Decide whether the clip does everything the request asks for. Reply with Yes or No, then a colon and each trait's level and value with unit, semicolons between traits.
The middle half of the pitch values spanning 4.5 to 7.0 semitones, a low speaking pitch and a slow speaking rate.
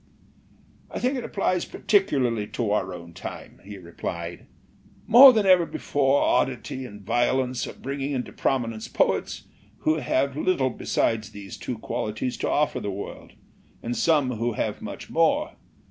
No: average, 5.3 semitones; low, 125 Hz; average, 155 wpm